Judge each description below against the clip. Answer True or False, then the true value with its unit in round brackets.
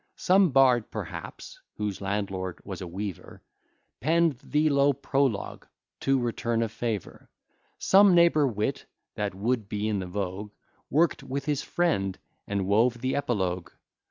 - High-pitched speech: False (115 Hz)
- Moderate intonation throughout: False (6.0 semitones)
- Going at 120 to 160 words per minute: True (140 wpm)